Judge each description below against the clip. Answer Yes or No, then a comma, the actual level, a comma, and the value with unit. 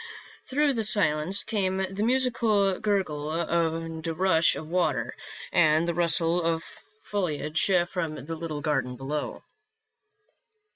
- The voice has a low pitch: No, medium, 170 Hz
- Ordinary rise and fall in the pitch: Yes, average, 3.9 semitones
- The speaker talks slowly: Yes, slow, 115 wpm